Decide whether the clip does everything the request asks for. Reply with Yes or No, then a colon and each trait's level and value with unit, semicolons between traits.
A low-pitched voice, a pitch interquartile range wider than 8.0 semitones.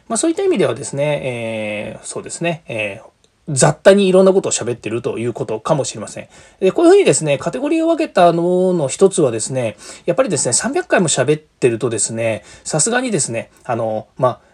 No: medium, 150 Hz; wide, 8.5 semitones